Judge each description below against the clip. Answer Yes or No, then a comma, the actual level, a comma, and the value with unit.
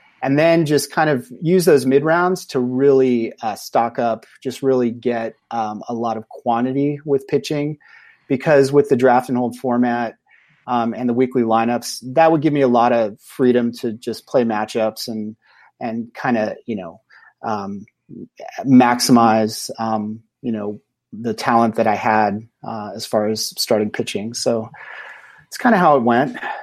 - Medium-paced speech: Yes, average, 175 wpm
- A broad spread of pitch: No, average, 3.2 semitones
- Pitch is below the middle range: Yes, low, 120 Hz